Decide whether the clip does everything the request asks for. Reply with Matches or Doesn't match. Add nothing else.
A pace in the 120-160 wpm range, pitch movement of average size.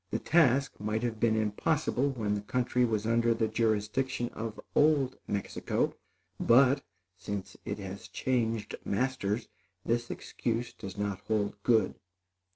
Matches